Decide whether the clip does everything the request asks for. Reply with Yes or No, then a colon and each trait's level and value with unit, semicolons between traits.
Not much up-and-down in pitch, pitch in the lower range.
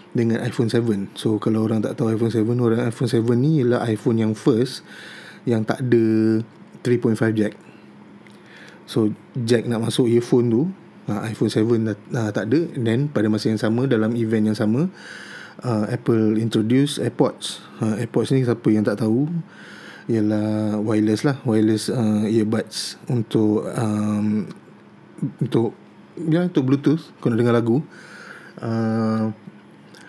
Yes: narrow, 2.0 semitones; low, 115 Hz